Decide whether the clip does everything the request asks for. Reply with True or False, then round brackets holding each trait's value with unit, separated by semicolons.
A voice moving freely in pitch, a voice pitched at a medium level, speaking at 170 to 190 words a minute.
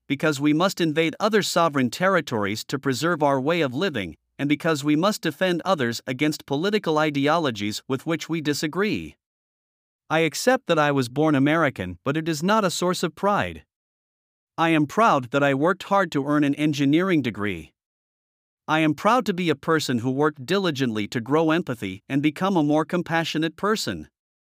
False (4.0 semitones; 155 Hz; 175 wpm)